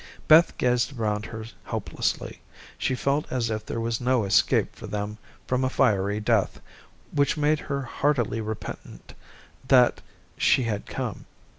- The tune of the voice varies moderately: Yes, average, 3.8 semitones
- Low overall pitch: Yes, low, 120 Hz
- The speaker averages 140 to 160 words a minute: Yes, average, 145 wpm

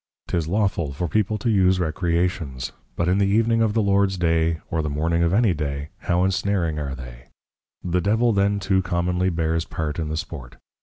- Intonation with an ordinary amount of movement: Yes, average, 3.7 semitones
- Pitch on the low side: Yes, very low, 90 Hz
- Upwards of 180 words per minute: Yes, average, 195 wpm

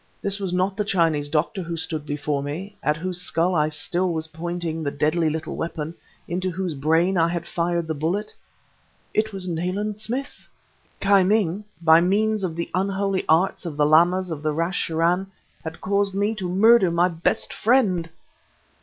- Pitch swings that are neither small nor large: Yes, average, 3.2 semitones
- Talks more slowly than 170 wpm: No, average, 175 wpm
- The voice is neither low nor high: Yes, medium, 175 Hz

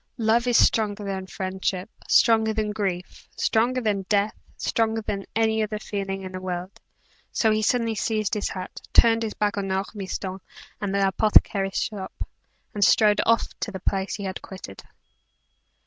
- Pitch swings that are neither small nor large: No, narrow, 2.3 semitones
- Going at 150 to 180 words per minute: Yes, average, 165 wpm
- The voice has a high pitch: Yes, high, 205 Hz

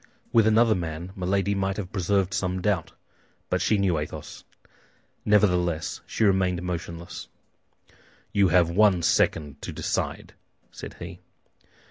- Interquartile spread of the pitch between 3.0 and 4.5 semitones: No, narrow, 2.5 semitones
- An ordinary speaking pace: No, slow, 125 wpm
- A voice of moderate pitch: No, very low, 95 Hz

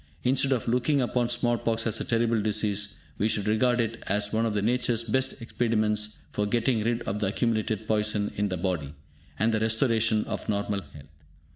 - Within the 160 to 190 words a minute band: Yes, average, 185 wpm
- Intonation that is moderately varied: No, narrow, 2.2 semitones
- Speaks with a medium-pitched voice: No, low, 110 Hz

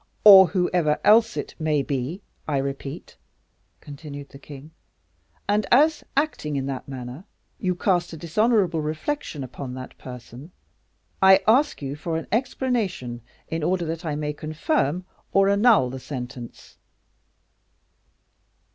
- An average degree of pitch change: No, wide, 5.9 semitones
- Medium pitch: Yes, medium, 160 Hz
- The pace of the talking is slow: Yes, slow, 130 wpm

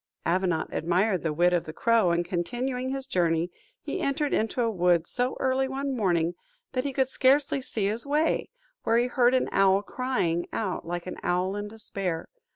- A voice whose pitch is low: No, high, 205 Hz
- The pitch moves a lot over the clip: Yes, wide, 6.6 semitones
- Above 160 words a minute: Yes, average, 185 wpm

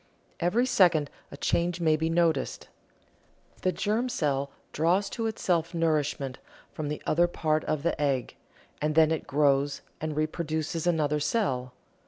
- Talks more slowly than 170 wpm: Yes, average, 145 wpm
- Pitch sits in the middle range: Yes, medium, 155 Hz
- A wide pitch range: No, average, 2.8 semitones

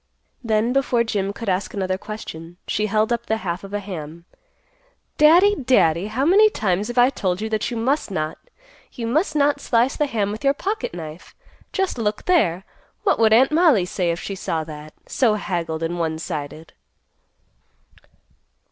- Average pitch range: No, wide, 7.0 semitones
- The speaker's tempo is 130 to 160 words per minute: No, average, 175 wpm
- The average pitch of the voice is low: No, high, 215 Hz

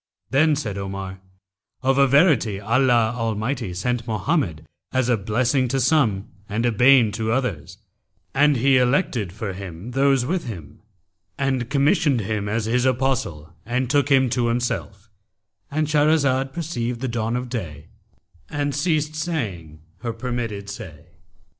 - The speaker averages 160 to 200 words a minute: No, average, 140 wpm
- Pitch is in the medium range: No, low, 120 Hz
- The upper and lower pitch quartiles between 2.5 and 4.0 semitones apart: No, average, 4.8 semitones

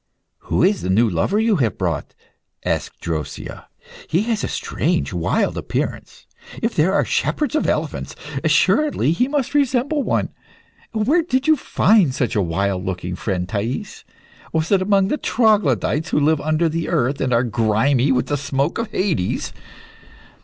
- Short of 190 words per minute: Yes, average, 160 wpm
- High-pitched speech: No, medium, 155 Hz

